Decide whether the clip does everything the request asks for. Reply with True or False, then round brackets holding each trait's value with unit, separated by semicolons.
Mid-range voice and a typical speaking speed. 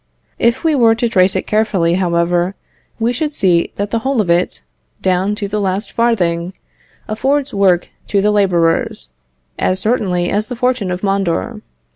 False (200 Hz; 165 wpm)